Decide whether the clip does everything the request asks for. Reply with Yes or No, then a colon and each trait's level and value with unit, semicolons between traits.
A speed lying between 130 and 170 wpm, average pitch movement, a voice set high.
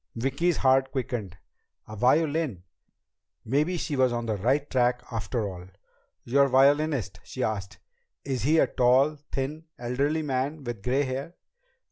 No: average, 140 wpm; average, 3.3 semitones; low, 130 Hz